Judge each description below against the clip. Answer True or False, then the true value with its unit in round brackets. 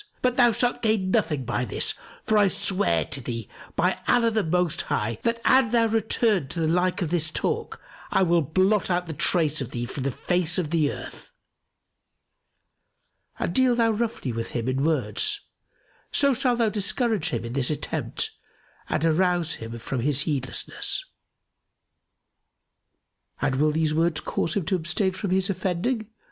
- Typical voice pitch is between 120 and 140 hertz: False (175 Hz)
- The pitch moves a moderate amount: False (6.8 semitones)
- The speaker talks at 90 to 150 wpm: False (165 wpm)